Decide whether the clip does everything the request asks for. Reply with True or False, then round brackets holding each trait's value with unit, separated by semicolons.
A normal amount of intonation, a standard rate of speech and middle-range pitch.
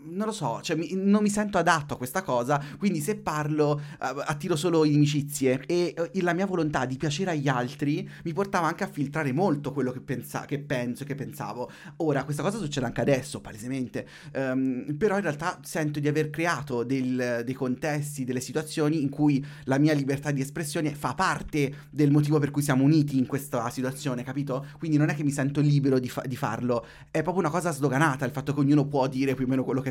False (3.3 semitones; 210 wpm; 145 Hz)